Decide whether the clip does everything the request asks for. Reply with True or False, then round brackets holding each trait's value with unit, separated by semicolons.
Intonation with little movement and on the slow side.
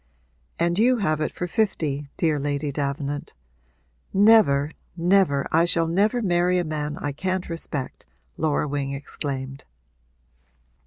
False (4.1 semitones; 125 wpm)